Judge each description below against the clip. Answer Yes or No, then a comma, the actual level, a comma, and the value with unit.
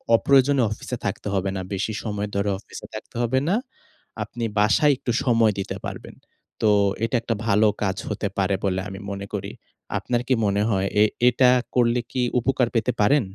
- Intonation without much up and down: No, average, 3.7 semitones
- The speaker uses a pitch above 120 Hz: No, low, 110 Hz